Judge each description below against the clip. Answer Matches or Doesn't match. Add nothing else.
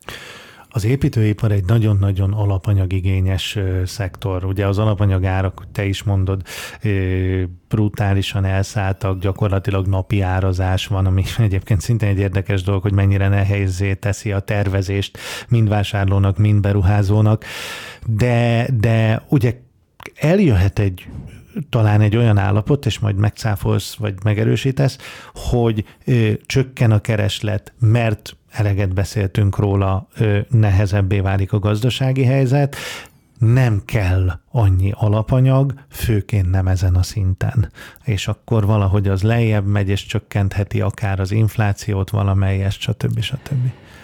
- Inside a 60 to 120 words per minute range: Matches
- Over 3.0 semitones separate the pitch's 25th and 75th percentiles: Doesn't match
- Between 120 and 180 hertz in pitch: Doesn't match